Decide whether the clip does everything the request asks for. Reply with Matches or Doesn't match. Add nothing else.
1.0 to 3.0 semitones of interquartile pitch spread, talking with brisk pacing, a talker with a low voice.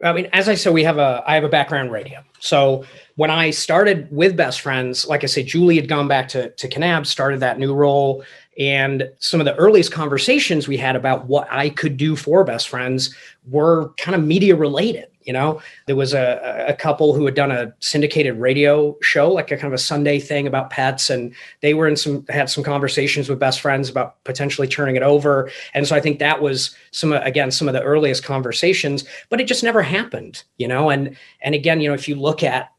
Doesn't match